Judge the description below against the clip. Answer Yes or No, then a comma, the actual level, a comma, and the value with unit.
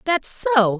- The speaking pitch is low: No, very high, 285 Hz